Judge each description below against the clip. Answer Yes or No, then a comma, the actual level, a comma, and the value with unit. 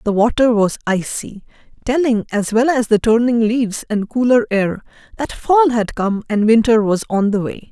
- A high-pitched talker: Yes, high, 230 Hz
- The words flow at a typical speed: Yes, average, 185 wpm